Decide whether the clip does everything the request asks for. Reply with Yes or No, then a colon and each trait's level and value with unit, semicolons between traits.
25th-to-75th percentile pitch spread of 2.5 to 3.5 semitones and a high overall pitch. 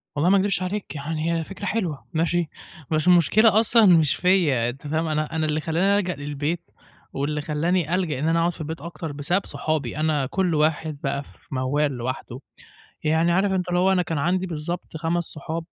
No: average, 3.1 semitones; medium, 160 Hz